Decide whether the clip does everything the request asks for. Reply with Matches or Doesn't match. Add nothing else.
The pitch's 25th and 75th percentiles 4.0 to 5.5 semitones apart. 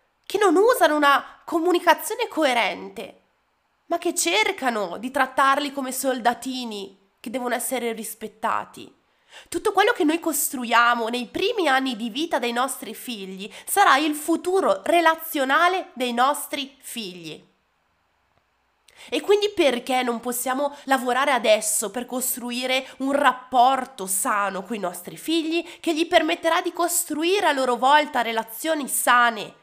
Matches